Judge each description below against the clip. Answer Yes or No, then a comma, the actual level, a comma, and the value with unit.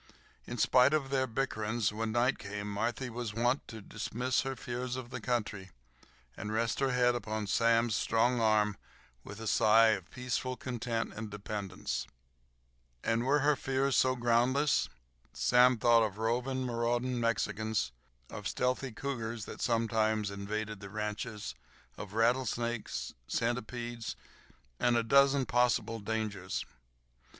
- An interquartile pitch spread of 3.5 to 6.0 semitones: No, narrow, 2.6 semitones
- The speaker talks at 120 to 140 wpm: Yes, slow, 135 wpm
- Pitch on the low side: Yes, low, 115 Hz